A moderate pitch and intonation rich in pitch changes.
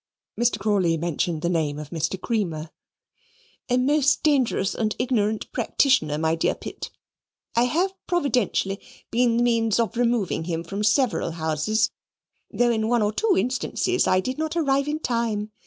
No: high, 220 Hz; wide, 6.1 semitones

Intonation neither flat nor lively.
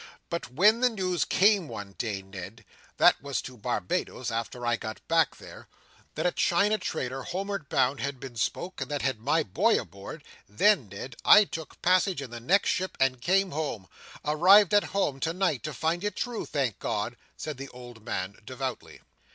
No: wide, 7.4 semitones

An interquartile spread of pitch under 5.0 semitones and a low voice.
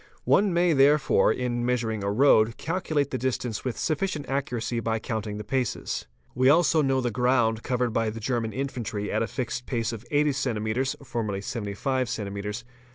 Yes: average, 3.4 semitones; low, 125 Hz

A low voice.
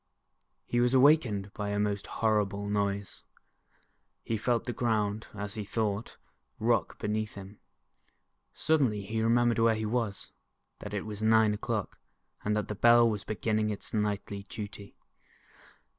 Yes: low, 105 Hz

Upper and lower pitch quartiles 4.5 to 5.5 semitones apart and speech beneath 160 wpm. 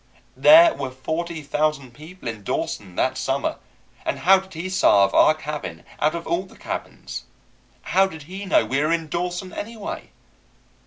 No: average, 5.2 semitones; average, 165 wpm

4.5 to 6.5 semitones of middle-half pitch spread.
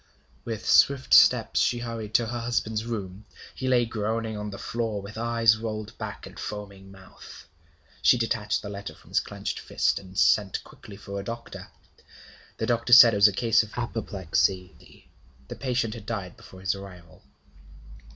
No: average, 2.7 semitones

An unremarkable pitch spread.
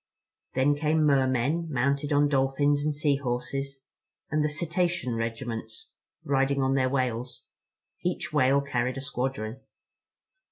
No: narrow, 2.3 semitones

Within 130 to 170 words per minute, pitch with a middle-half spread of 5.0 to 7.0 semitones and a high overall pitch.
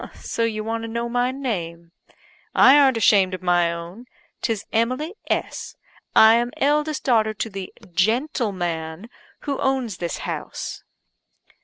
Yes: average, 140 wpm; wide, 5.4 semitones; high, 225 Hz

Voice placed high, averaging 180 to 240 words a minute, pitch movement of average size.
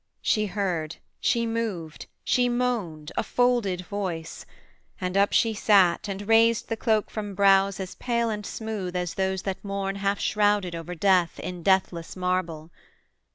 No: high, 195 Hz; average, 155 wpm; average, 3.2 semitones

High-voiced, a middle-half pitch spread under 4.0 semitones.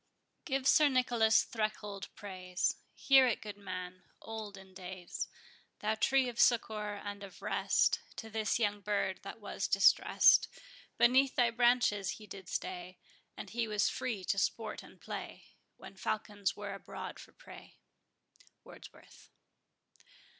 Yes: high, 210 Hz; average, 3.3 semitones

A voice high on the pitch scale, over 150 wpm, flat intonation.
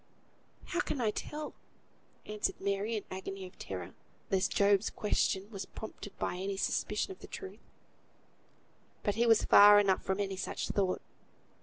Yes: high, 200 Hz; average, 160 wpm; narrow, 1.9 semitones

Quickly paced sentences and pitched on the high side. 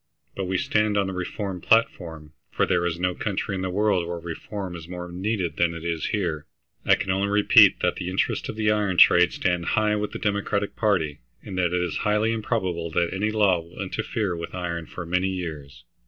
No: fast, 215 wpm; very low, 90 Hz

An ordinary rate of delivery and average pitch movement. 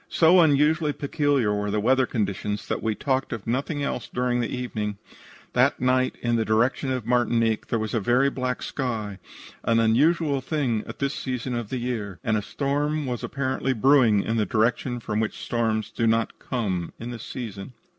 Yes: average, 185 wpm; average, 3.4 semitones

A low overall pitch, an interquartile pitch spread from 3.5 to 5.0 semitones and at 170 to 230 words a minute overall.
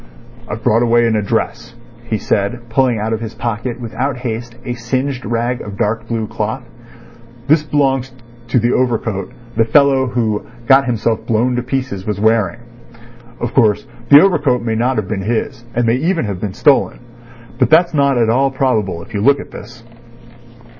No: low, 120 Hz; average, 3.1 semitones; average, 180 wpm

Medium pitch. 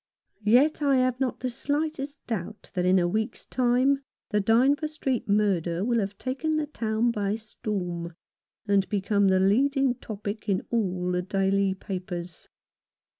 No: high, 215 Hz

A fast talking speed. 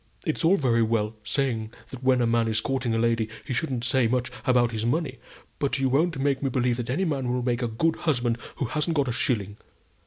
Yes: fast, 230 wpm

